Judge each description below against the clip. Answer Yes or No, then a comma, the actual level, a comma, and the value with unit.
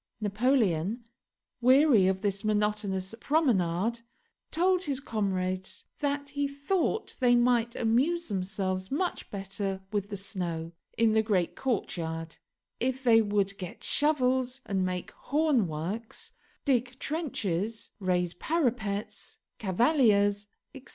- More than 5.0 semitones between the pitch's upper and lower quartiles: Yes, wide, 5.5 semitones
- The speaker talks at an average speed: No, slow, 110 wpm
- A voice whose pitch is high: Yes, high, 215 Hz